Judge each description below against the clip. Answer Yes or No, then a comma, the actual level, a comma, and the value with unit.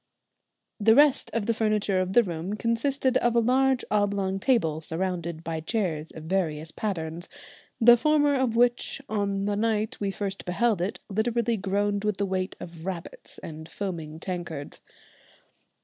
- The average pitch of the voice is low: No, high, 200 Hz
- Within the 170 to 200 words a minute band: No, average, 155 wpm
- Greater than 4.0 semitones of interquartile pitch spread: Yes, average, 4.9 semitones